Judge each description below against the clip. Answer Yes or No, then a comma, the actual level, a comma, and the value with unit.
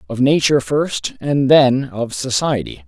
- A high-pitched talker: No, low, 130 Hz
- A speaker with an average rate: Yes, average, 145 wpm